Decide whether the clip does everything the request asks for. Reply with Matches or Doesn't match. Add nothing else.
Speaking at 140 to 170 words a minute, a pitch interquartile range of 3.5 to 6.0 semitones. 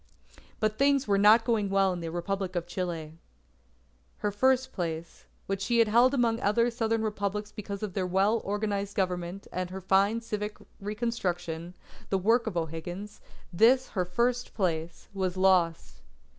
Matches